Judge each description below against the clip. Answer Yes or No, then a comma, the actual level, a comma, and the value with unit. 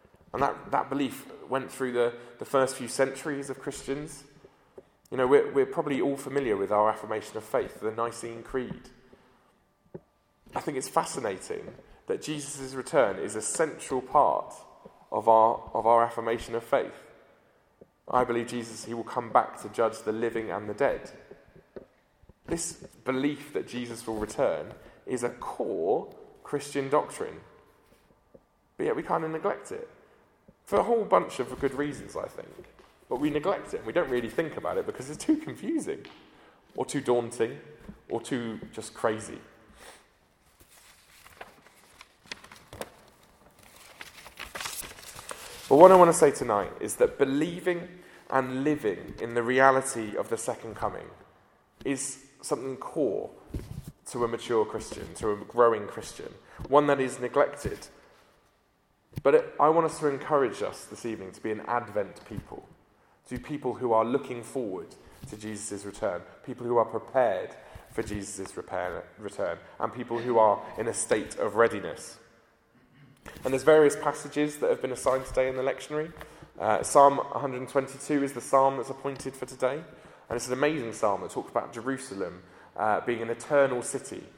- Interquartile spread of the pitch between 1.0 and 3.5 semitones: No, average, 4.1 semitones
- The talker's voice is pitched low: Yes, low, 130 Hz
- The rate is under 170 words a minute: Yes, average, 155 wpm